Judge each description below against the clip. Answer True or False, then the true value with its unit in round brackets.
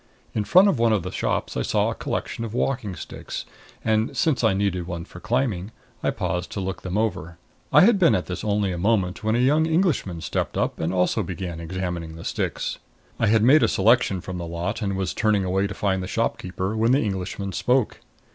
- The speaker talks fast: True (220 wpm)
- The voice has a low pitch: True (100 Hz)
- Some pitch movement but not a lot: True (4.0 semitones)